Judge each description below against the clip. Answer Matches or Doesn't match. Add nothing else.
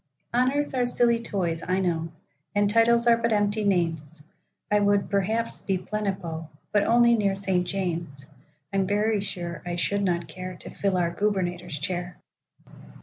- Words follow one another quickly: Doesn't match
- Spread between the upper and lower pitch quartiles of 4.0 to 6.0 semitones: Doesn't match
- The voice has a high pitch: Matches